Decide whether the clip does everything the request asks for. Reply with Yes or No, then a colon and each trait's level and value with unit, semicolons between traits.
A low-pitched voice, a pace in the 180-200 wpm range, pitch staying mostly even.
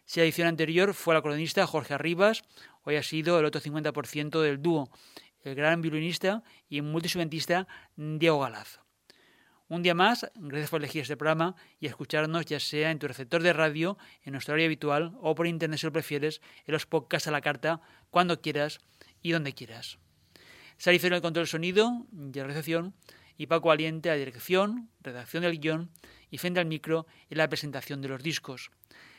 No: medium, 160 Hz; average, 185 wpm; narrow, 2.3 semitones